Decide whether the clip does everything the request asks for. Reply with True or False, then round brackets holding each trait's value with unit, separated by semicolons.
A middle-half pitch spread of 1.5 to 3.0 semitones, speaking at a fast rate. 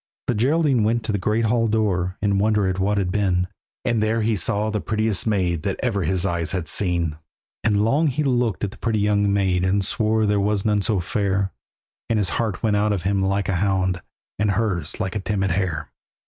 True (2.6 semitones; 220 wpm)